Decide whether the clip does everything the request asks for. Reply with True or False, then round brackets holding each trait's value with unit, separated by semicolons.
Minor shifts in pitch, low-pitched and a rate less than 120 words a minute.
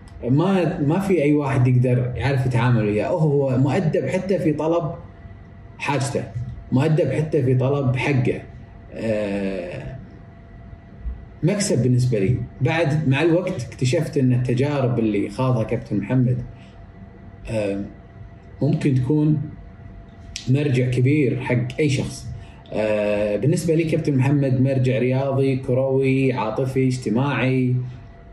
False (4.5 semitones; 130 Hz; 110 wpm)